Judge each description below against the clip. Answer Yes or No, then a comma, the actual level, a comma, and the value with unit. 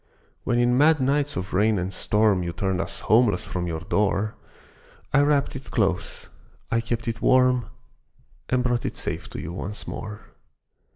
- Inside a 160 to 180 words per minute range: Yes, average, 170 wpm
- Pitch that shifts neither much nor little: Yes, average, 4.6 semitones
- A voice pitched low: Yes, low, 110 Hz